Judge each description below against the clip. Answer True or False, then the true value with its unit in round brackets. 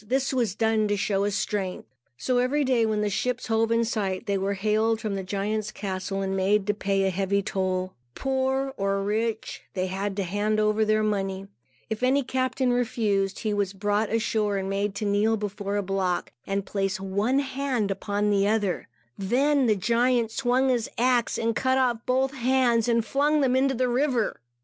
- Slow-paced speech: False (190 wpm)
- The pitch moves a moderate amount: True (3.9 semitones)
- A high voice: True (215 Hz)